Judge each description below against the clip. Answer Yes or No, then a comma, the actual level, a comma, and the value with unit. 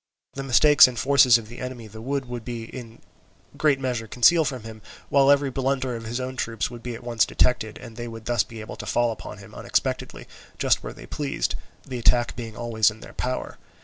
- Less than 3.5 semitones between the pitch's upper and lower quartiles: Yes, narrow, 2.4 semitones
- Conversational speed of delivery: No, fast, 220 wpm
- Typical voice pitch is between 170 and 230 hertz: No, low, 120 Hz